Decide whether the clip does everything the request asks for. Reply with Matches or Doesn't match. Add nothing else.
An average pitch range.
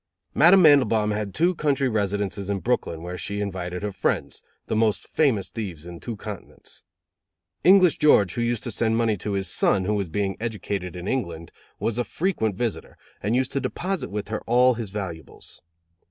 Matches